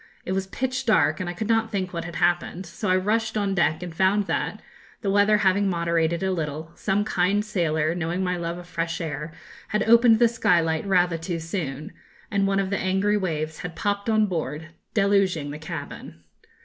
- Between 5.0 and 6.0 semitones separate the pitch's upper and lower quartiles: No, average, 3.4 semitones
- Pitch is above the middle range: No, medium, 180 Hz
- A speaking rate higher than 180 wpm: Yes, average, 200 wpm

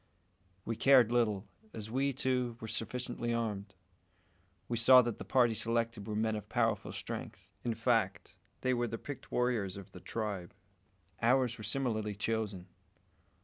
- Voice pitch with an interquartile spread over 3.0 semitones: No, narrow, 2.5 semitones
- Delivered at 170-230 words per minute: No, average, 150 wpm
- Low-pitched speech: Yes, low, 115 Hz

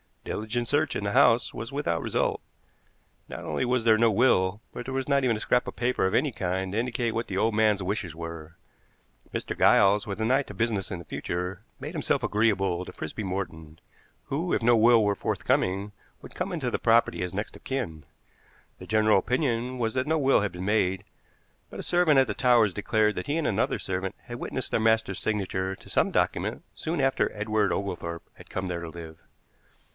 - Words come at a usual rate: No, fast, 210 wpm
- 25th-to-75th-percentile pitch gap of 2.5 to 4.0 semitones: No, average, 4.4 semitones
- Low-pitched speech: Yes, low, 110 Hz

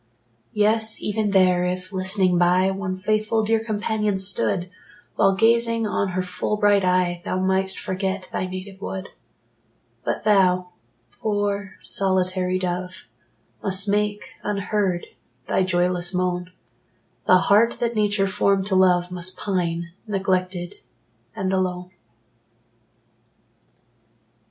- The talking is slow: Yes, slow, 115 wpm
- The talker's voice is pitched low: No, high, 190 Hz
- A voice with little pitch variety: Yes, narrow, 2.1 semitones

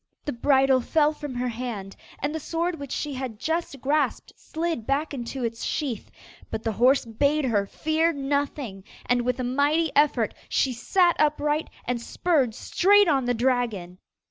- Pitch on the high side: Yes, very high, 270 Hz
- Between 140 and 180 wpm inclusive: Yes, average, 170 wpm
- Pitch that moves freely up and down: No, average, 3.9 semitones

